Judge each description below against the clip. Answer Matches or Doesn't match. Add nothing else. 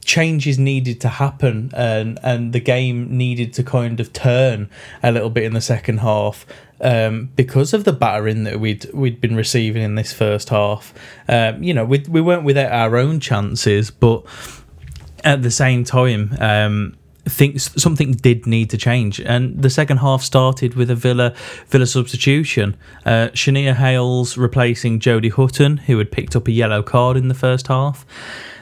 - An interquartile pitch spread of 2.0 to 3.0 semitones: Matches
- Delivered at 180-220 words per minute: Doesn't match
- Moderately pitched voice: Doesn't match